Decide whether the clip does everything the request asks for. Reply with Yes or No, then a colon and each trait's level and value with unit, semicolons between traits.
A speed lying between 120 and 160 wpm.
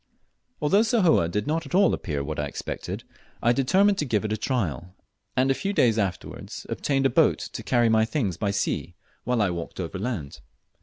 No: average, 195 wpm